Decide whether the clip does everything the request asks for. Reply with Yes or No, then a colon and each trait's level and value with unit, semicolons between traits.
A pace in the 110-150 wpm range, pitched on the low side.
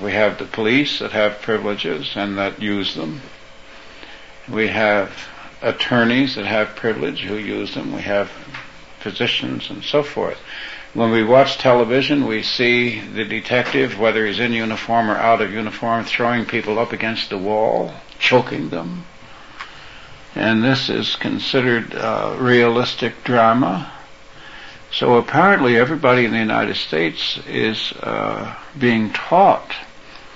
Yes: slow, 135 wpm; low, 115 Hz